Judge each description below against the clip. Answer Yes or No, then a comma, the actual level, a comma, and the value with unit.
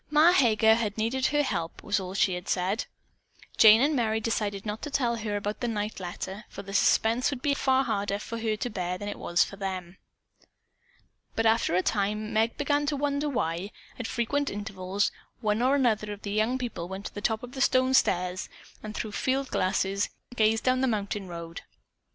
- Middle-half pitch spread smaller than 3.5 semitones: No, average, 4.0 semitones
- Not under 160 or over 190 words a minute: No, fast, 205 wpm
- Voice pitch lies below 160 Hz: No, high, 215 Hz